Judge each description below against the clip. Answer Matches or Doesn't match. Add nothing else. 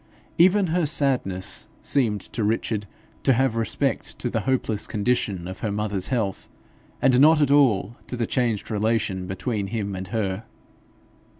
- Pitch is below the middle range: Matches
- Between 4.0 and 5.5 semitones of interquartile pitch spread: Matches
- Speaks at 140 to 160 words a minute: Matches